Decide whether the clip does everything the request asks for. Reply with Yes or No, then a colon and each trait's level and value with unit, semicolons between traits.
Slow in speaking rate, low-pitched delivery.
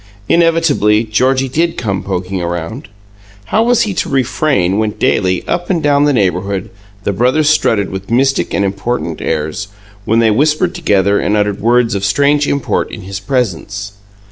No: average, 165 wpm; low, 110 Hz